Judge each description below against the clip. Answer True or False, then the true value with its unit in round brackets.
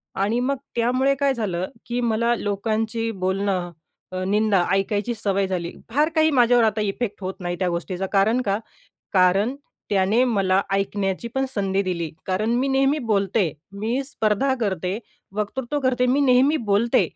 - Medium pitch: False (210 Hz)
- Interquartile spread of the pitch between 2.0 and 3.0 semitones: False (4.2 semitones)